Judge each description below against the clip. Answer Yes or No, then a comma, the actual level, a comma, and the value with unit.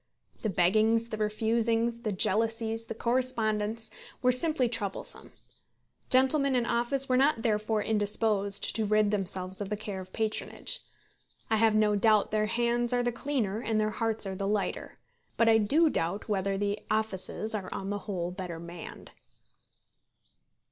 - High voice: Yes, high, 215 Hz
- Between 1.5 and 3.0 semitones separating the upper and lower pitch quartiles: Yes, narrow, 2.4 semitones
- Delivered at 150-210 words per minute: Yes, average, 155 wpm